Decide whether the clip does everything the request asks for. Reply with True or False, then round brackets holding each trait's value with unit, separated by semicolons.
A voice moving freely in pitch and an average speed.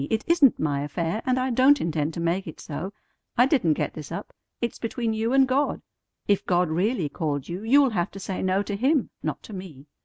False (7.1 semitones; 220 wpm)